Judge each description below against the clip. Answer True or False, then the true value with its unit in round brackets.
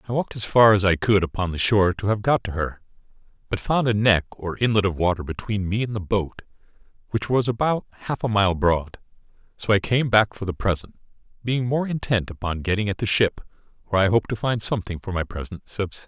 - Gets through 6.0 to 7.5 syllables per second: True (6.1 syllables/s)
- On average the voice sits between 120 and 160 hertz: False (105 Hz)